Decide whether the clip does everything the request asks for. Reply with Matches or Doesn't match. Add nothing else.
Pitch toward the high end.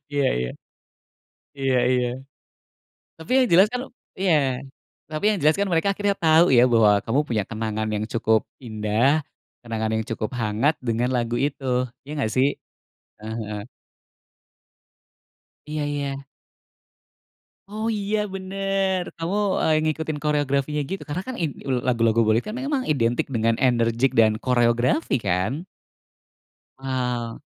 Doesn't match